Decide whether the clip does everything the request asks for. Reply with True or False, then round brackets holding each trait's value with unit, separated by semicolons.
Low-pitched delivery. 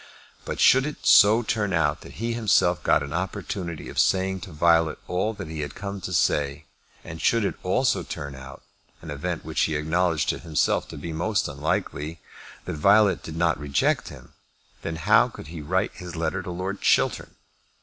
True (85 Hz)